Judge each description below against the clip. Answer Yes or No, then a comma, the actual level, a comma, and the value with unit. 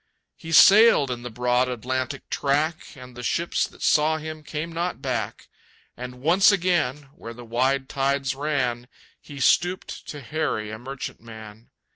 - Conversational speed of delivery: Yes, average, 150 wpm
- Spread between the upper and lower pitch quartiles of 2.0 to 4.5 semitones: Yes, average, 4.2 semitones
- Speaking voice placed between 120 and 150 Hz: Yes, low, 135 Hz